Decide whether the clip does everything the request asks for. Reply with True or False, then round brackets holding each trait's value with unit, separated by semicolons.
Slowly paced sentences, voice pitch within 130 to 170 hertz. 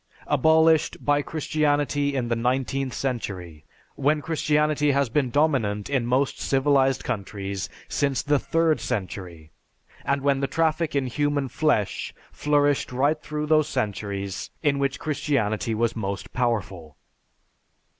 True (125 wpm; 135 Hz)